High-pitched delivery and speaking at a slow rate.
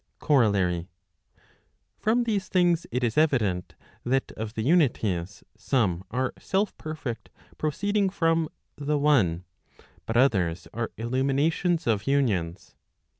No: low, 130 Hz; slow, 115 wpm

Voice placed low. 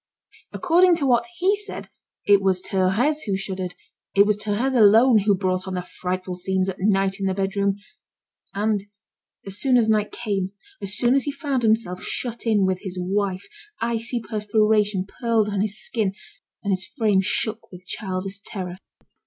No: high, 205 Hz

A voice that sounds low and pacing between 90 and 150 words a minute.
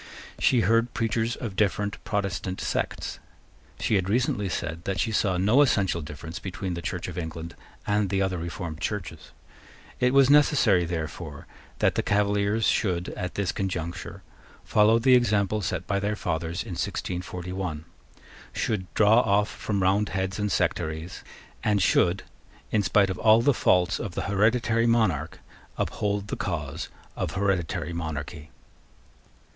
Yes: very low, 95 Hz; average, 145 wpm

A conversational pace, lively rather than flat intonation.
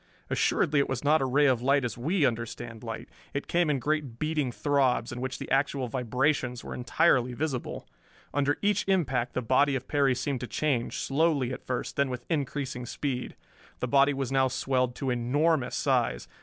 No: average, 185 wpm; average, 2.7 semitones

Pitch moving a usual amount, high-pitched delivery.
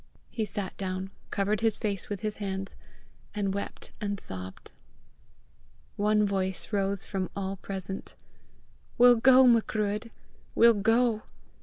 No: narrow, 2.1 semitones; high, 200 Hz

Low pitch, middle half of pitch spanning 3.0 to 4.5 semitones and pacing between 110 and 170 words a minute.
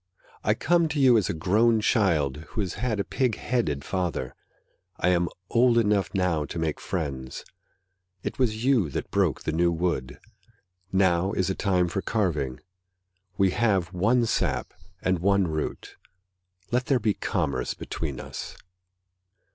No: very low, 95 Hz; wide, 5.5 semitones; average, 155 wpm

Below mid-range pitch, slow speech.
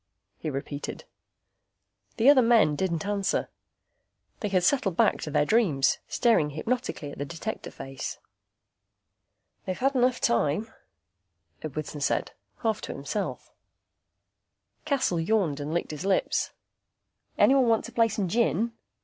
No: high, 190 Hz; slow, 130 wpm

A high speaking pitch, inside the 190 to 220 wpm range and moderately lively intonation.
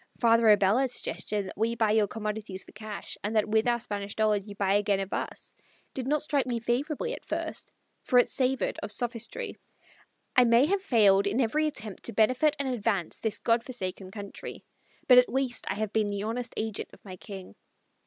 Yes: high, 220 Hz; average, 195 wpm; average, 3.4 semitones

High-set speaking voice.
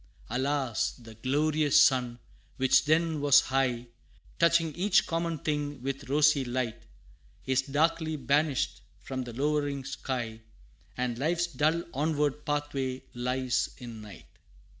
No: medium, 140 Hz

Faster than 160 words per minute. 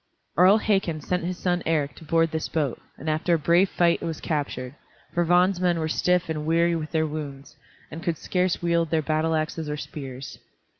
Yes: fast, 205 wpm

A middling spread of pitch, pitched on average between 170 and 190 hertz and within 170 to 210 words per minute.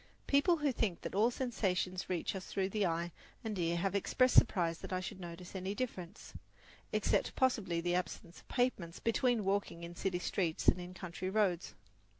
Yes: average, 3.8 semitones; medium, 185 Hz; average, 185 wpm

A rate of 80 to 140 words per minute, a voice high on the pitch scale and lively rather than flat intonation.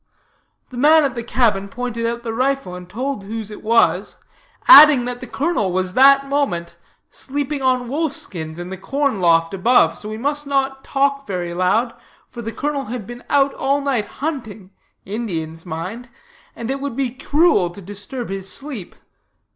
No: average, 175 wpm; high, 240 Hz; wide, 6.1 semitones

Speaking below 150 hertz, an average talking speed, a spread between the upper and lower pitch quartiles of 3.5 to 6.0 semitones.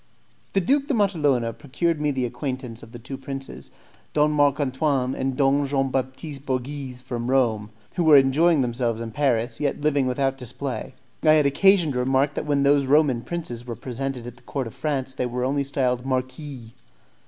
No: low, 135 Hz; average, 190 wpm; narrow, 2.6 semitones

